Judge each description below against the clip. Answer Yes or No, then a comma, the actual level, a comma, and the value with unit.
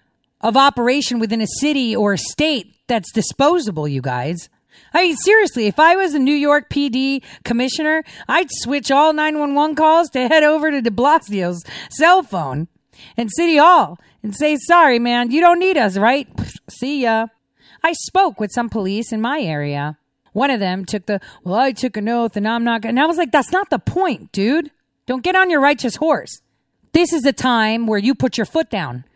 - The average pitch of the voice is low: No, very high, 255 Hz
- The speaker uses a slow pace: No, average, 200 wpm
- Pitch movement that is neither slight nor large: No, wide, 6.1 semitones